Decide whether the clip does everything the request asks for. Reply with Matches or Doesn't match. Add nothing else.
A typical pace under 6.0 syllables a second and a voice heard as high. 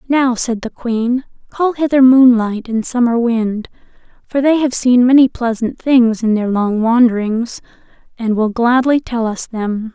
Matches